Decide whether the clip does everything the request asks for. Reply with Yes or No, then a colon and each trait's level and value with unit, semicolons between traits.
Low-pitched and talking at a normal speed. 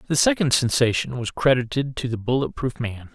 Yes: low, 125 Hz; average, 190 wpm